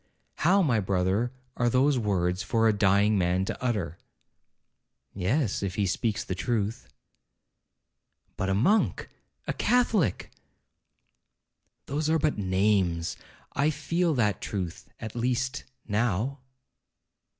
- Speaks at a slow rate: Yes, slow, 110 wpm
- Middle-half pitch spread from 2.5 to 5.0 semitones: No, wide, 5.6 semitones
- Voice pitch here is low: Yes, low, 110 Hz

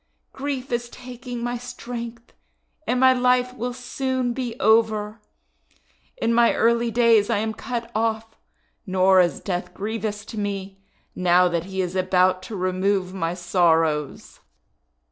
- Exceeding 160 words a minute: No, average, 140 wpm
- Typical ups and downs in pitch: Yes, average, 4.5 semitones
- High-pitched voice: Yes, high, 220 Hz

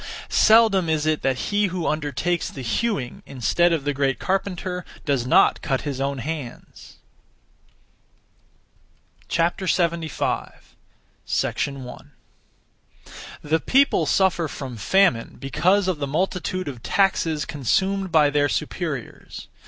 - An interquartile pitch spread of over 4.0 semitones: Yes, average, 5.0 semitones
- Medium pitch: Yes, medium, 160 Hz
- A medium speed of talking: No, slow, 115 wpm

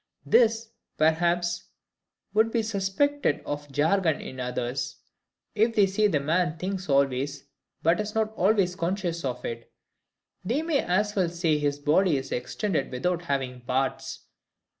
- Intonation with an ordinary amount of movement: No, wide, 6.4 semitones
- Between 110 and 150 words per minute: Yes, average, 140 wpm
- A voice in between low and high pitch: Yes, medium, 175 Hz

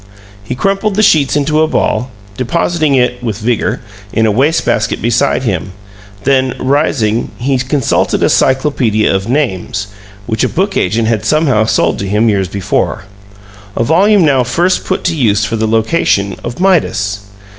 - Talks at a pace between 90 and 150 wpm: No, average, 165 wpm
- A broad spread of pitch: Yes, wide, 5.8 semitones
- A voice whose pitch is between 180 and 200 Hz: No, low, 125 Hz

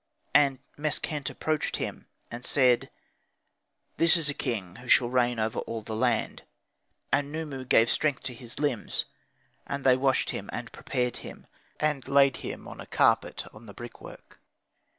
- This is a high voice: No, low, 130 Hz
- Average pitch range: Yes, average, 3.2 semitones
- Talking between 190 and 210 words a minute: No, average, 160 wpm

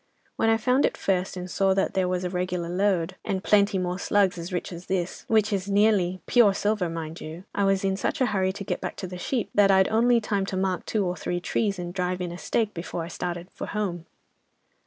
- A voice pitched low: No, high, 190 Hz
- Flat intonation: Yes, narrow, 2.3 semitones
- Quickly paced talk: Yes, fast, 240 wpm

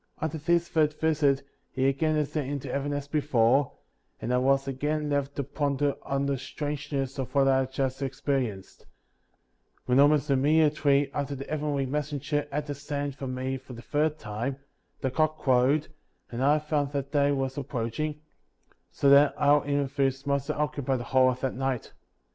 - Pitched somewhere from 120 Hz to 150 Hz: Yes, medium, 140 Hz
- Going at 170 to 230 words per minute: Yes, average, 180 wpm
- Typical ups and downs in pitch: No, narrow, 1.8 semitones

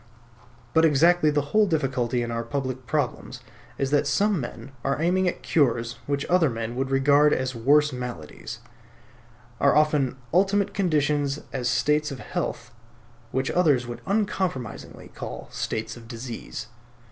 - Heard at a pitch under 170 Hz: Yes, medium, 140 Hz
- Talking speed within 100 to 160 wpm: Yes, average, 145 wpm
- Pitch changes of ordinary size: Yes, average, 3.9 semitones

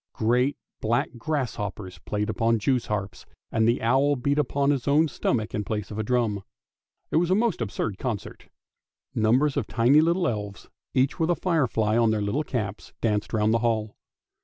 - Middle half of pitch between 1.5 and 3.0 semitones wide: No, average, 4.7 semitones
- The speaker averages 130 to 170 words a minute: No, average, 185 wpm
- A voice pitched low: Yes, low, 115 Hz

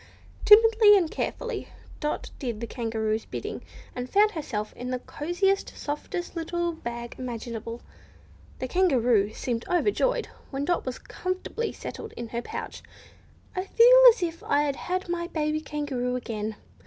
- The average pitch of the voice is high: Yes, very high, 295 Hz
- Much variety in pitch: Yes, wide, 7.4 semitones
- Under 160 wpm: Yes, average, 145 wpm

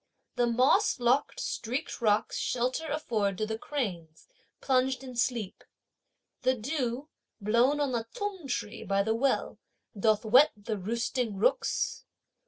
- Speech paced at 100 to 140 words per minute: Yes, slow, 135 wpm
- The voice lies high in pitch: Yes, high, 240 Hz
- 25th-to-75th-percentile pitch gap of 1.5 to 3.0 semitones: No, average, 3.7 semitones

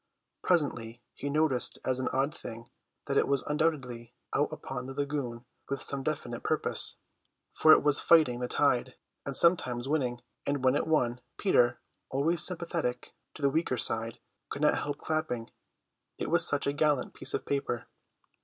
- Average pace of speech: Yes, average, 165 wpm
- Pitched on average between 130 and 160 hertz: Yes, medium, 140 Hz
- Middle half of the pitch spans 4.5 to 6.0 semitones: No, average, 3.5 semitones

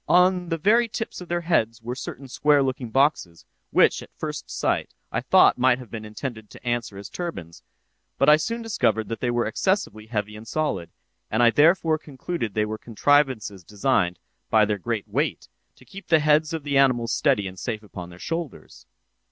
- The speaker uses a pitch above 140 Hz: No, low, 125 Hz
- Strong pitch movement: Yes, wide, 6.5 semitones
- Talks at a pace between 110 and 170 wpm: No, average, 195 wpm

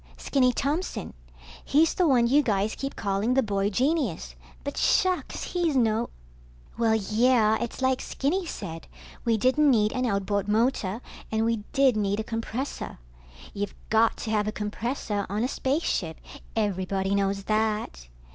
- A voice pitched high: Yes, high, 220 Hz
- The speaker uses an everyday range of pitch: Yes, average, 4.3 semitones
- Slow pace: No, average, 150 wpm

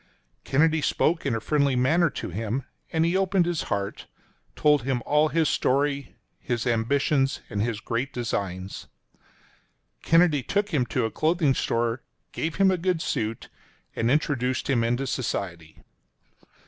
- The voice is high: No, low, 135 Hz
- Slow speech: No, average, 150 wpm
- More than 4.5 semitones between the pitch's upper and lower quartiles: Yes, wide, 5.5 semitones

